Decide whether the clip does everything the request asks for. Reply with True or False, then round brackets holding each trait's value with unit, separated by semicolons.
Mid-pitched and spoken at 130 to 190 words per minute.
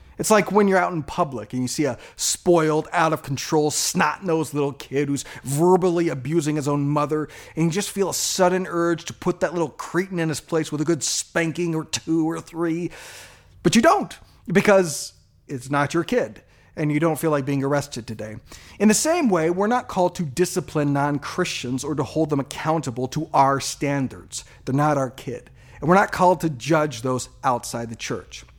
False (155 Hz; 205 wpm)